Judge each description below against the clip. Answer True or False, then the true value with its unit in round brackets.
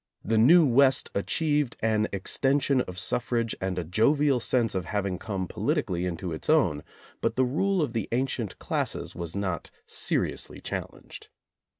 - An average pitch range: False (6.4 semitones)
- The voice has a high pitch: False (115 Hz)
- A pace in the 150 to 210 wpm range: True (155 wpm)